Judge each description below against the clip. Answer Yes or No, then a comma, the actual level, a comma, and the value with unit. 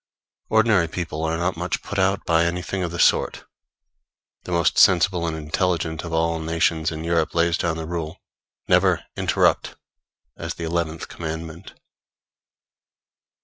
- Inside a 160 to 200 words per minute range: No, average, 145 wpm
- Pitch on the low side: Yes, very low, 85 Hz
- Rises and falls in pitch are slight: Yes, narrow, 1.4 semitones